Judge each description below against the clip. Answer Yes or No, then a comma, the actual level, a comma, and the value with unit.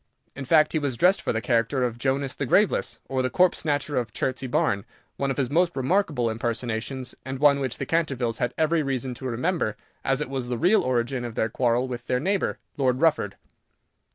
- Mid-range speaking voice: No, low, 130 Hz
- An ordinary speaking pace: No, fast, 210 wpm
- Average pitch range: Yes, average, 3.3 semitones